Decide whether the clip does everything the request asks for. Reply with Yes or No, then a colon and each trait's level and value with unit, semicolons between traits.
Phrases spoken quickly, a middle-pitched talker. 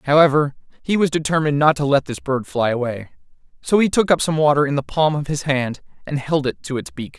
Yes: fast, 240 wpm; medium, 145 Hz